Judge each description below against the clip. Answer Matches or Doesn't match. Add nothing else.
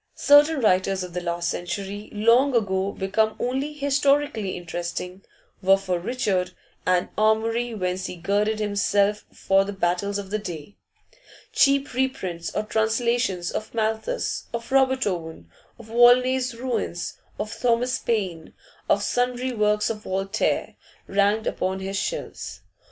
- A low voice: Doesn't match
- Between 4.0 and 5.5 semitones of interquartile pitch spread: Matches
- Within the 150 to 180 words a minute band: Doesn't match